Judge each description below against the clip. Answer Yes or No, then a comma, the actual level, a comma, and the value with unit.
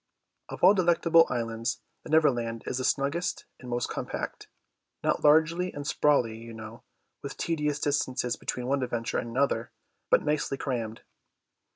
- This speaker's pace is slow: No, average, 150 wpm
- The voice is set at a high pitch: No, low, 135 Hz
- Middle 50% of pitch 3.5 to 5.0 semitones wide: Yes, average, 4.4 semitones